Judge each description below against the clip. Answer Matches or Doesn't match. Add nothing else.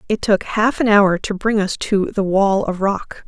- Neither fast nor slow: Doesn't match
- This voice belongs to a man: Doesn't match